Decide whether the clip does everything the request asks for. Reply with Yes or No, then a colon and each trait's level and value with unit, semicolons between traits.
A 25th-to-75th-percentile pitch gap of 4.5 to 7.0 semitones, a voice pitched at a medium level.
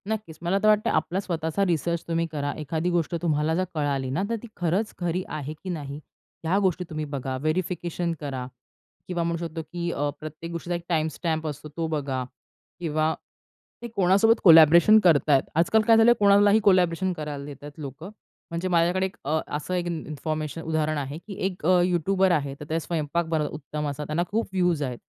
No: average, 3.1 semitones; medium, 165 Hz